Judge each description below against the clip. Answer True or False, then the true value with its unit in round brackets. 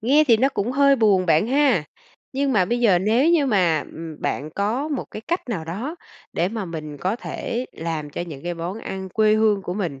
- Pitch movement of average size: False (6.5 semitones)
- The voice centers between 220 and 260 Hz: False (205 Hz)